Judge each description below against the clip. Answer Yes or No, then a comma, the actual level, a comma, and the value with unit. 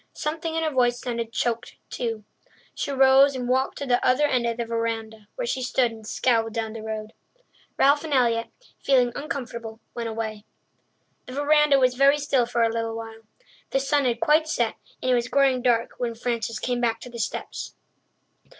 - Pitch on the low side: No, high, 245 Hz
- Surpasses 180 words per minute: Yes, average, 190 wpm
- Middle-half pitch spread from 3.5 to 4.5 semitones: No, average, 3.0 semitones